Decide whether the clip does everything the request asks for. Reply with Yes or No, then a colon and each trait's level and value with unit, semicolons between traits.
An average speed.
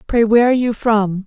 No: fast, 235 wpm